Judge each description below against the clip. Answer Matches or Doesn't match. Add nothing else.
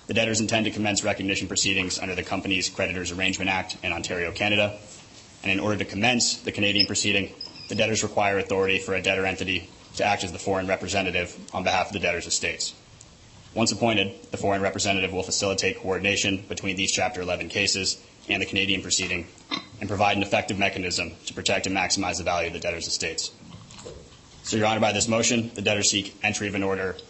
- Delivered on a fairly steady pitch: Matches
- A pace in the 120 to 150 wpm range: Doesn't match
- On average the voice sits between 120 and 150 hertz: Doesn't match